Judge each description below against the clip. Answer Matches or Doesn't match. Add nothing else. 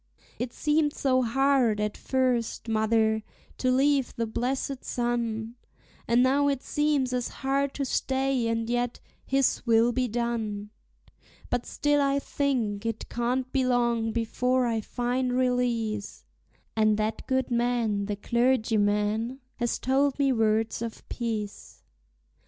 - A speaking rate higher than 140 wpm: Doesn't match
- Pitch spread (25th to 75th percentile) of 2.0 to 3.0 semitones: Matches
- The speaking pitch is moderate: Doesn't match